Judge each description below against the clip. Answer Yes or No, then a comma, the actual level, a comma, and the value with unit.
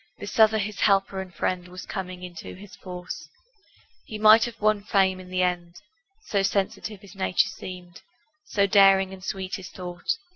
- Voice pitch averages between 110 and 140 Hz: No, high, 190 Hz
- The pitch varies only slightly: Yes, narrow, 2.0 semitones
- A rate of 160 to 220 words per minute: Yes, average, 175 wpm